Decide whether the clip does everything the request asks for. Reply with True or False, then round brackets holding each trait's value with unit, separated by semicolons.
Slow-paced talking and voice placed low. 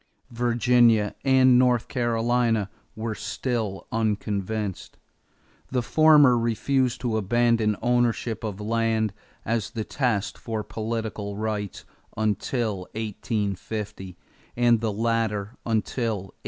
True (100 wpm; 115 Hz)